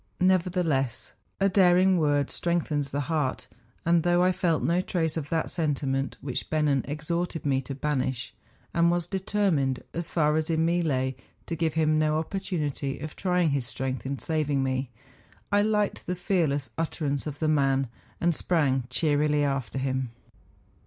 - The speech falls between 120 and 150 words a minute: No, average, 165 wpm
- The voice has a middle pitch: Yes, medium, 155 Hz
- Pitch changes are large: No, average, 3.8 semitones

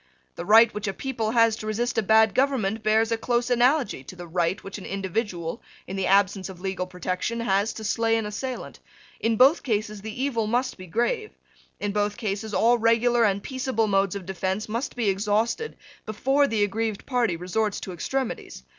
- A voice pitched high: Yes, high, 215 Hz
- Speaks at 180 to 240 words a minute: Yes, average, 190 wpm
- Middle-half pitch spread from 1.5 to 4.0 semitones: Yes, average, 3.2 semitones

